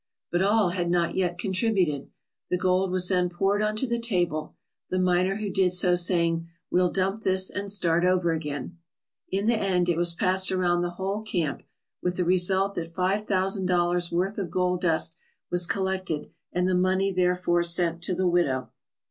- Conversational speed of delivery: Yes, average, 185 wpm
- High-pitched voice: No, medium, 180 Hz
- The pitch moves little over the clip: Yes, narrow, 1.7 semitones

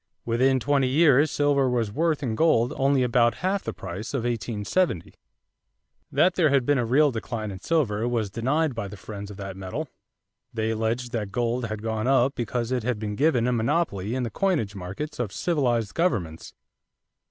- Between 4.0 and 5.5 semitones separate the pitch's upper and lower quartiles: Yes, average, 4.5 semitones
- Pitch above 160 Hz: No, low, 120 Hz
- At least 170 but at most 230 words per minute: Yes, average, 185 wpm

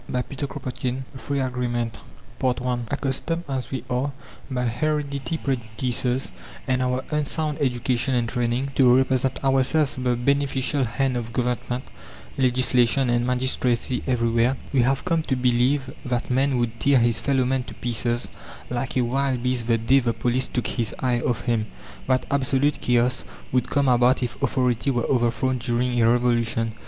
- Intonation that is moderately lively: No, narrow, 1.8 semitones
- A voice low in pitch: Yes, low, 125 Hz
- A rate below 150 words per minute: No, average, 155 wpm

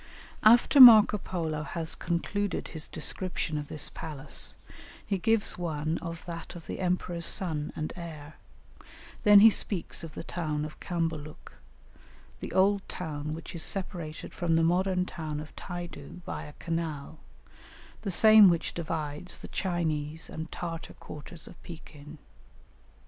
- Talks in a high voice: No, medium, 165 Hz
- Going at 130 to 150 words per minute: Yes, average, 145 wpm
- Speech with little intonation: No, average, 3.0 semitones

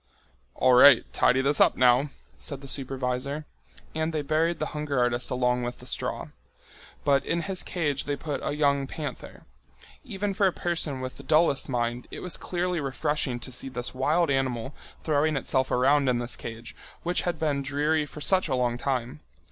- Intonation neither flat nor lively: Yes, average, 3.6 semitones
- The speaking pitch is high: No, medium, 140 Hz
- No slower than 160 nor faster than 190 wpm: Yes, average, 185 wpm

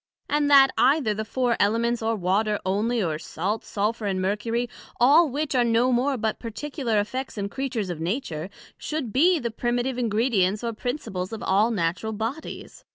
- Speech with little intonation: No, average, 4.0 semitones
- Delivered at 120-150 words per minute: No, average, 170 wpm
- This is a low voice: No, high, 230 Hz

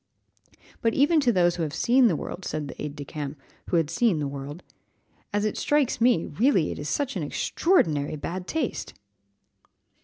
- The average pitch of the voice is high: No, medium, 175 Hz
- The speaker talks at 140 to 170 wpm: No, average, 180 wpm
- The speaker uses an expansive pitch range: Yes, wide, 8.3 semitones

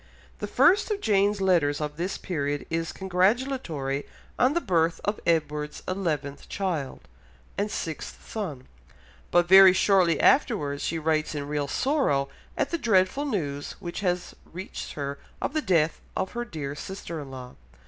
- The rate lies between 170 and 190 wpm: No, average, 155 wpm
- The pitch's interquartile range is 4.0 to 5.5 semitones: Yes, average, 5.1 semitones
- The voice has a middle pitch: Yes, medium, 170 Hz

